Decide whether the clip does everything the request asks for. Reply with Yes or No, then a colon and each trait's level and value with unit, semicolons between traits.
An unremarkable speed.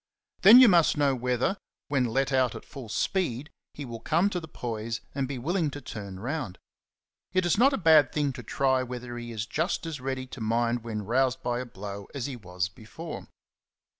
No: fast, 210 wpm